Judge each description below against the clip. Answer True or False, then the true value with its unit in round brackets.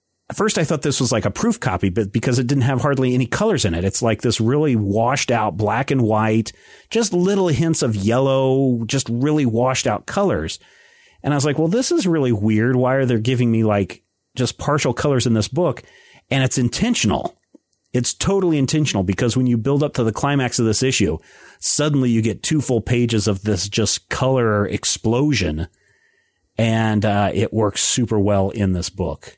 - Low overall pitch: True (120 Hz)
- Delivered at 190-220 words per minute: True (200 wpm)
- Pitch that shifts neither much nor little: True (4.2 semitones)